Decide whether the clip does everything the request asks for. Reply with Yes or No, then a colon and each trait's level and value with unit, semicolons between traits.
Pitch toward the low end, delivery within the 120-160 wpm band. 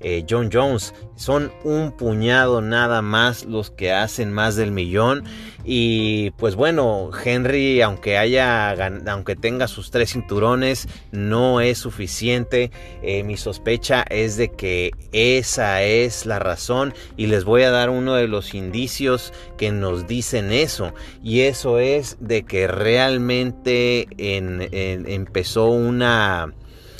Yes: low, 115 Hz; average, 135 wpm